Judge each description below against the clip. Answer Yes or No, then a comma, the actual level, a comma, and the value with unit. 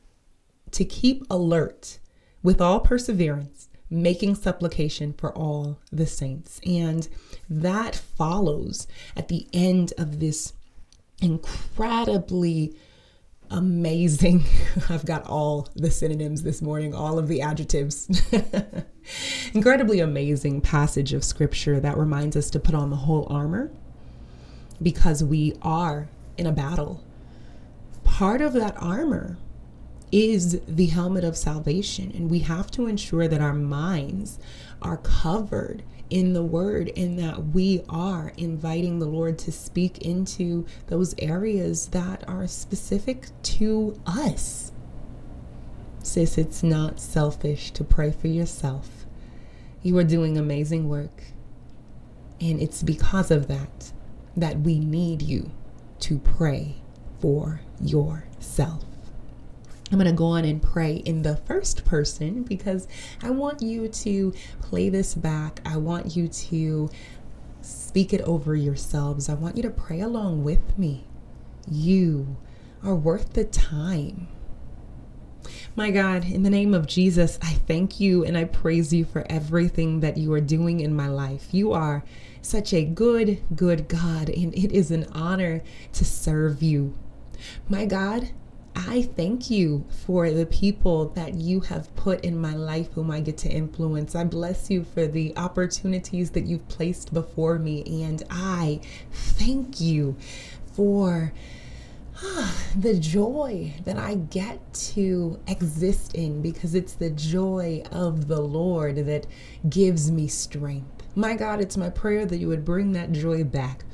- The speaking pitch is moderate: Yes, medium, 165 Hz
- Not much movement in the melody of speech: No, average, 3.3 semitones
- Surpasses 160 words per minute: No, average, 140 wpm